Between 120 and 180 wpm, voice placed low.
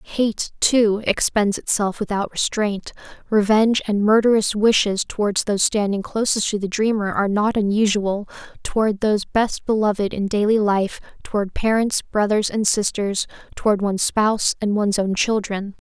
No: average, 150 wpm; high, 210 Hz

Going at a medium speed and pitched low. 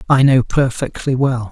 Yes: average, 160 wpm; low, 130 Hz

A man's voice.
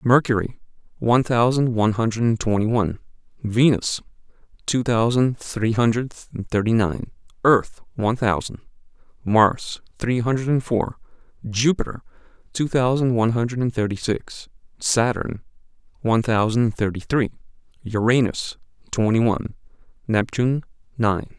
Yes: male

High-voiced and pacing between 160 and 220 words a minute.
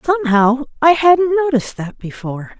No: very high, 275 Hz; average, 140 wpm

